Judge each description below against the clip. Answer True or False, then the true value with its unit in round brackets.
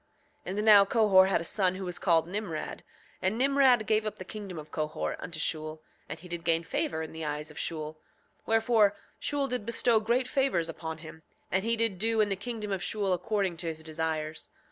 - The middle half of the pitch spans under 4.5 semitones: False (5.2 semitones)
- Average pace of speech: False (210 wpm)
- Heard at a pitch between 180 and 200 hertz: True (190 Hz)